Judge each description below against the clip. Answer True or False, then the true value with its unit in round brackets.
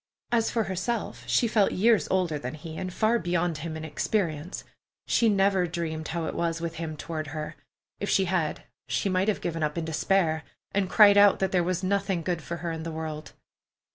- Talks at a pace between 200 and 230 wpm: True (205 wpm)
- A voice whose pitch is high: False (175 Hz)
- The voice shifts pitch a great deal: False (3.5 semitones)